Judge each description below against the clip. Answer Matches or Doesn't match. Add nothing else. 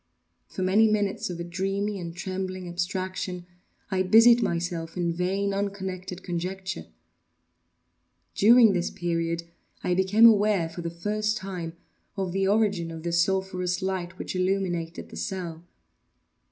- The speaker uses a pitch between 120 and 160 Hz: Doesn't match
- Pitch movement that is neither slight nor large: Doesn't match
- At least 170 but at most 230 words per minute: Doesn't match